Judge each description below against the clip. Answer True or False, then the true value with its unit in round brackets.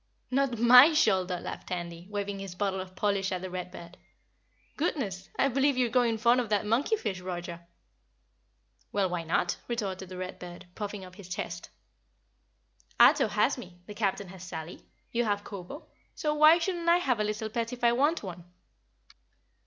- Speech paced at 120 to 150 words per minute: False (175 wpm)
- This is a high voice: True (205 Hz)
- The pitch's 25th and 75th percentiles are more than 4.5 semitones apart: True (5.0 semitones)